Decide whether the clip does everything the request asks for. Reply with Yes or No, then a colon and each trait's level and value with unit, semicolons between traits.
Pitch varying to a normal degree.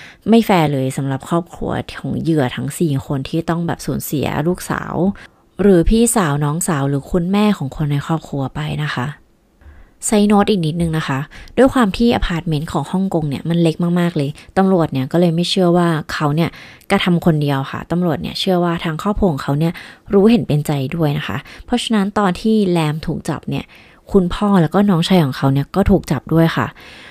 Yes: average, 4.6 semitones